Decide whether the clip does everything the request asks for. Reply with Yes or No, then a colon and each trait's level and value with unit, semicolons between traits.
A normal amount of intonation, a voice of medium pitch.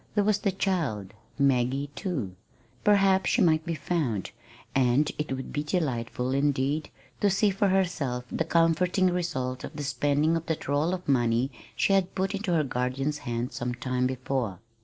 No: wide, 5.9 semitones; medium, 145 Hz